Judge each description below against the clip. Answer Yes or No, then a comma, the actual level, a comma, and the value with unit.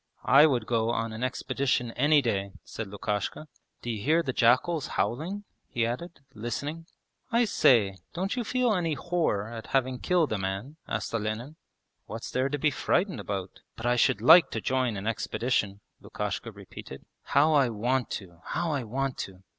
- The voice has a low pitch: Yes, low, 125 Hz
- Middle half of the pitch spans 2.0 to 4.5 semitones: No, wide, 5.6 semitones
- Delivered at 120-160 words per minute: No, average, 170 wpm